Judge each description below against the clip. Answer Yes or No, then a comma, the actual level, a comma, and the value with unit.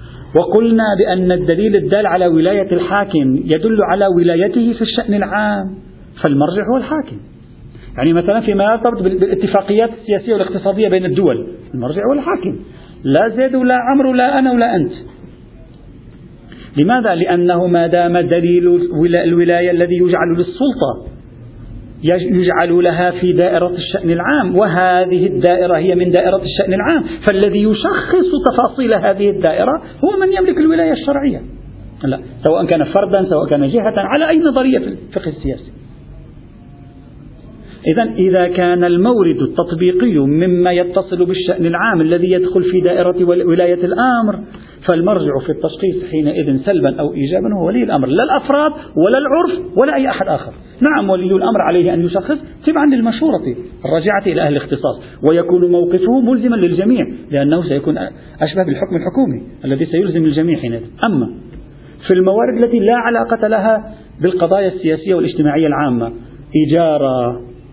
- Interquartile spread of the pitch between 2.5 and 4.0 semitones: No, average, 4.7 semitones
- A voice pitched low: No, medium, 185 Hz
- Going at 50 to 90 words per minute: No, fast, 135 wpm